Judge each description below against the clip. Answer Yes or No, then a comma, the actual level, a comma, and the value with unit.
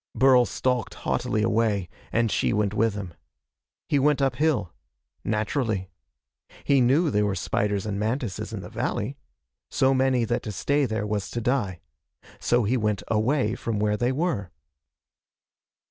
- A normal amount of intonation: Yes, average, 4.0 semitones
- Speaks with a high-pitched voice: No, low, 115 Hz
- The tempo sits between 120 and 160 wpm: Yes, average, 150 wpm